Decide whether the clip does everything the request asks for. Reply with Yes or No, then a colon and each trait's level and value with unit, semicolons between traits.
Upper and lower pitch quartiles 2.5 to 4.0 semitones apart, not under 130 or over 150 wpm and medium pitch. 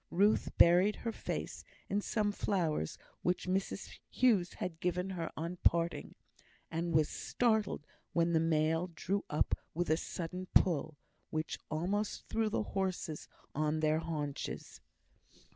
Yes: average, 3.4 semitones; slow, 135 wpm; medium, 175 Hz